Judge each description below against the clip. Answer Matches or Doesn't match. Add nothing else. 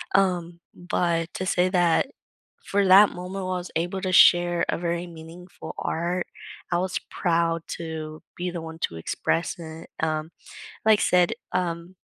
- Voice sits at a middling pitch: Matches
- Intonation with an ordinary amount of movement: Doesn't match